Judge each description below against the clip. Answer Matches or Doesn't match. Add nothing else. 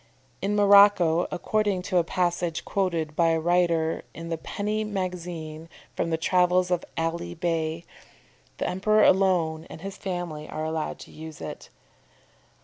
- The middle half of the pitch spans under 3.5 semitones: Matches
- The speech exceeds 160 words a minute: Doesn't match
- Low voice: Doesn't match